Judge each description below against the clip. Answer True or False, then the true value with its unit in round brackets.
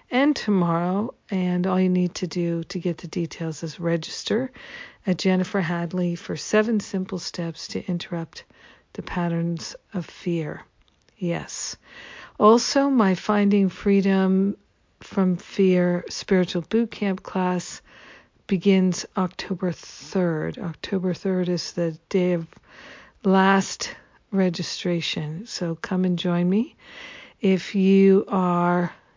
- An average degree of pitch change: False (2.2 semitones)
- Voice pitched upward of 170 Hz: True (185 Hz)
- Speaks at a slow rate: True (115 wpm)